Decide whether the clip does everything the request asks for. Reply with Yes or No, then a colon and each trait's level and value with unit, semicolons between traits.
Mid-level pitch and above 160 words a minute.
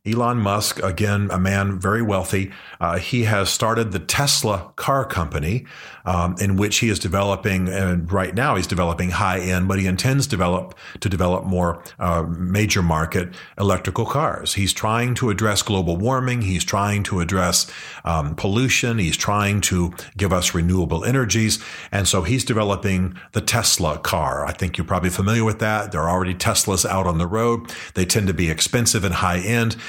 No: very low, 95 Hz; average, 180 wpm